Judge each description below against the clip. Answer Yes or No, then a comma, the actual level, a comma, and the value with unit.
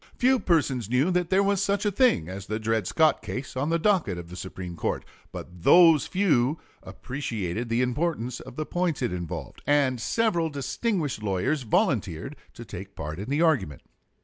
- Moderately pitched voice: No, low, 130 Hz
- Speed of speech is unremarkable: Yes, average, 175 wpm